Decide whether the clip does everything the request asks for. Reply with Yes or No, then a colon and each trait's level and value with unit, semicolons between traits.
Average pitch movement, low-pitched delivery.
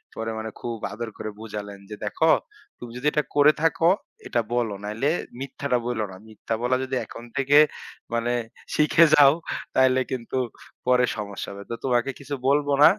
Yes: average, 3.8 semitones; low, 125 Hz